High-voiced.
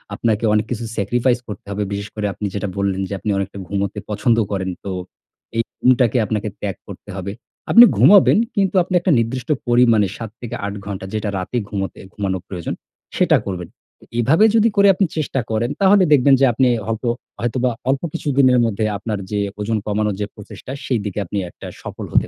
No: low, 110 Hz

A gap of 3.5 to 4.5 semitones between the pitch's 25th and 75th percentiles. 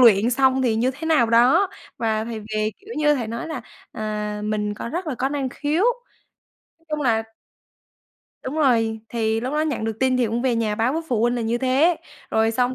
Yes: average, 3.8 semitones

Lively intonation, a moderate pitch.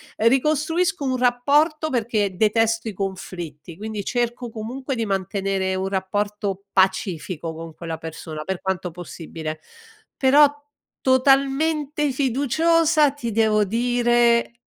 No: wide, 6.0 semitones; high, 225 Hz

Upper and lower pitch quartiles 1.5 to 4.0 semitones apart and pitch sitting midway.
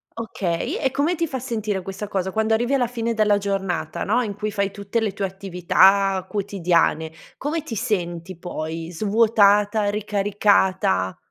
No: average, 2.8 semitones; high, 200 Hz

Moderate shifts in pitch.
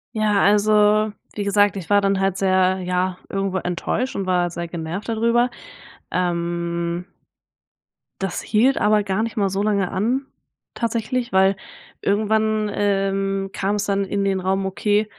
No: narrow, 2.1 semitones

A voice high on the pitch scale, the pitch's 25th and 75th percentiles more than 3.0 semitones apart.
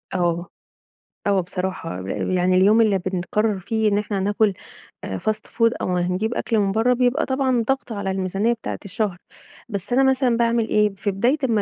Yes: high, 210 Hz; average, 3.7 semitones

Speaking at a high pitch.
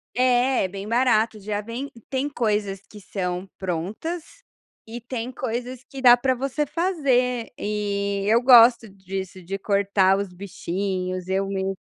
Yes: high, 215 Hz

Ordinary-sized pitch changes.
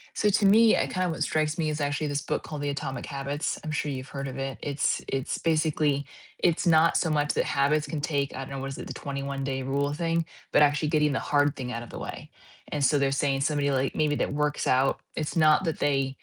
No: narrow, 2.0 semitones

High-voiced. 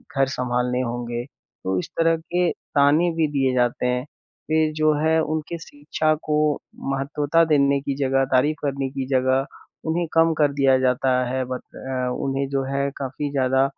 No: medium, 140 Hz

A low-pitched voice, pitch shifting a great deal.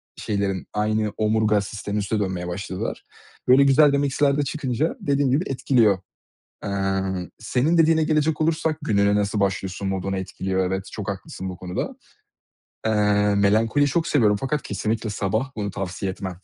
Yes: low, 105 Hz; wide, 6.2 semitones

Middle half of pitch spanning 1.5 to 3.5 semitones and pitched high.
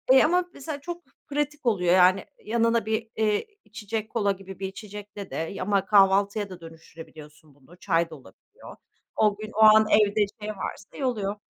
Yes: average, 2.9 semitones; high, 205 Hz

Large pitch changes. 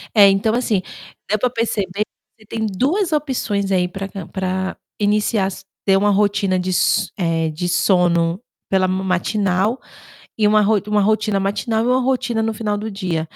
No: average, 2.7 semitones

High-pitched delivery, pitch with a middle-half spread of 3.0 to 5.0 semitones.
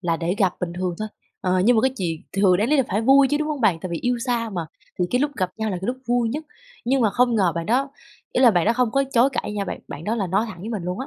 No: high, 220 Hz; wide, 5.4 semitones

